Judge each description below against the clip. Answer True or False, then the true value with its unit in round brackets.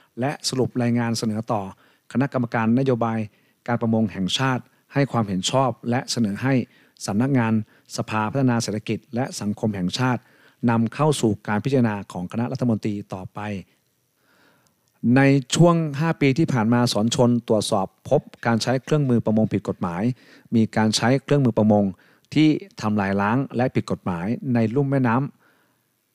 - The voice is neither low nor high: False (120 Hz)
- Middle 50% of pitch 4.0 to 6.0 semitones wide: False (3.4 semitones)